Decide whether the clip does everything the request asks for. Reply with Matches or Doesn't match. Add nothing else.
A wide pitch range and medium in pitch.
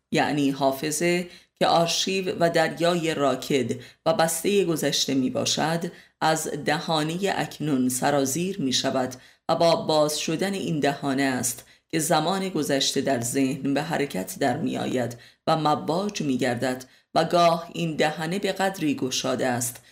Doesn't match